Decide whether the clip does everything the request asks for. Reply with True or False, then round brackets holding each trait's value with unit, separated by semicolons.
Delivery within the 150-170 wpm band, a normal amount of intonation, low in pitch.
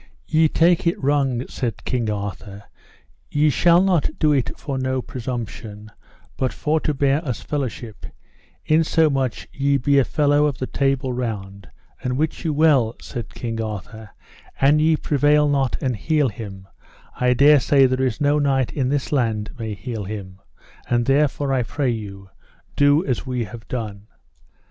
True (165 wpm; 4.3 semitones; 130 Hz)